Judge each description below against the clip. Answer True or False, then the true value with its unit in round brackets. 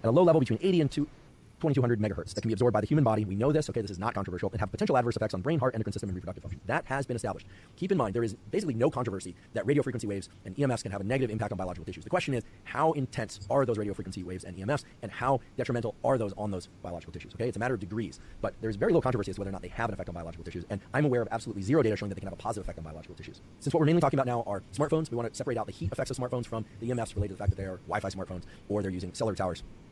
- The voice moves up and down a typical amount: True (4.8 semitones)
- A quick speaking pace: True (325 wpm)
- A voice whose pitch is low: True (110 Hz)